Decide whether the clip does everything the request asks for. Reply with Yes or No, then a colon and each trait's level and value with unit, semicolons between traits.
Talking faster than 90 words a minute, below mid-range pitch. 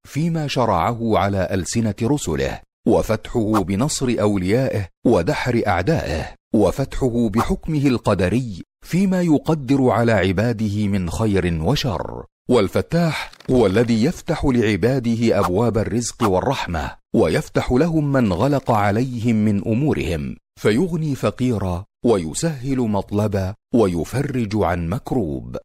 Yes: average, 100 wpm; low, 115 Hz